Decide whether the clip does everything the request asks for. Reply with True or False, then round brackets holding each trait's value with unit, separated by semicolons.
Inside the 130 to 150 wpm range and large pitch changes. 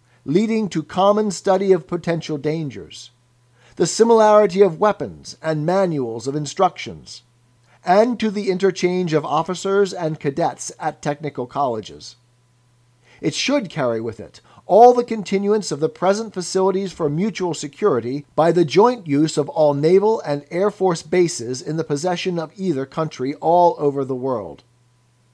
True (145 wpm; 6.1 semitones)